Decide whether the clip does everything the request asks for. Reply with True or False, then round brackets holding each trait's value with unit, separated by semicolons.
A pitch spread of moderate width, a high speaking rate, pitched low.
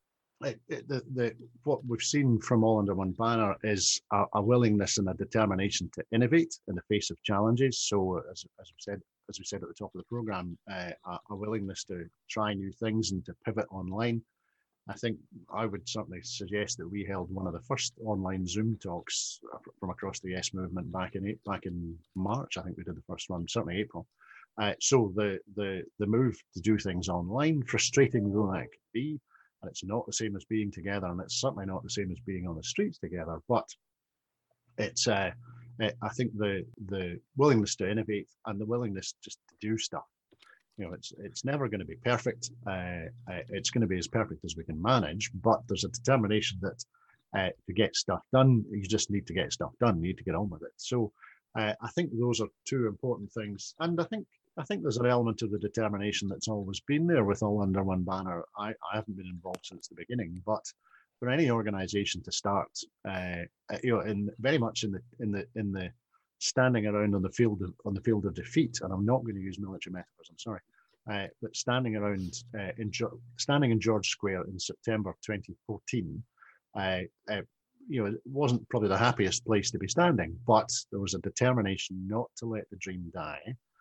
True (3.7 semitones; 210 wpm; 105 Hz)